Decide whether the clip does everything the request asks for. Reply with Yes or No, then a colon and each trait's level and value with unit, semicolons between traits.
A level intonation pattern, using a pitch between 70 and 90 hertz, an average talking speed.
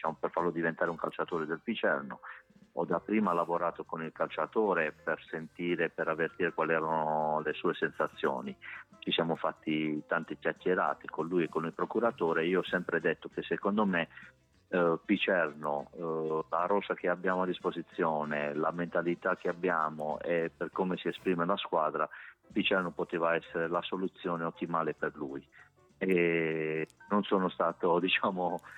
Yes: narrow, 2.1 semitones; very low, 85 Hz; average, 150 wpm